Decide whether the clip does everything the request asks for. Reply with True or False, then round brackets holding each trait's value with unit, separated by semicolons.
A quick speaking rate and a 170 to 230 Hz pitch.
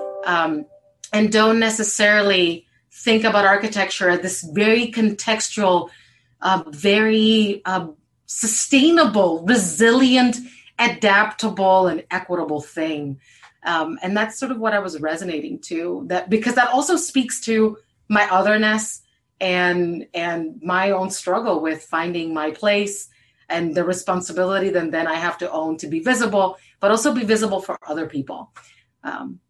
False (135 wpm; 190 Hz)